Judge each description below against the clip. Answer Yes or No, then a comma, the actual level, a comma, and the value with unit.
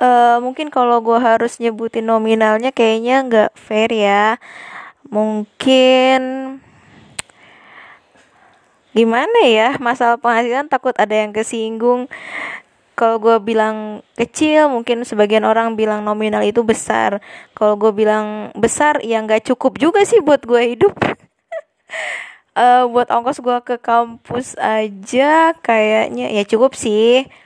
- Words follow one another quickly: No, average, 120 wpm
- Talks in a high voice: Yes, high, 235 Hz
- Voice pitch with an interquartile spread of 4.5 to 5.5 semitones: No, average, 2.9 semitones